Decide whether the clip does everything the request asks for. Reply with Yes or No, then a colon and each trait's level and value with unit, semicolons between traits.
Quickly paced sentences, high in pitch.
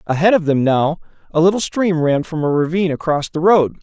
No: fast, 220 wpm; medium, 165 Hz